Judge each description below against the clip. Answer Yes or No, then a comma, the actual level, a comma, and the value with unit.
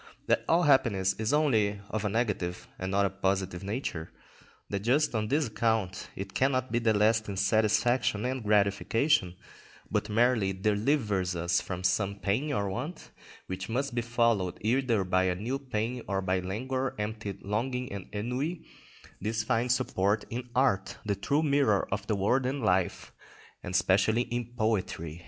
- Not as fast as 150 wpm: No, average, 155 wpm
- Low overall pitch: Yes, low, 110 Hz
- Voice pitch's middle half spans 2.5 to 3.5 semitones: No, average, 4.2 semitones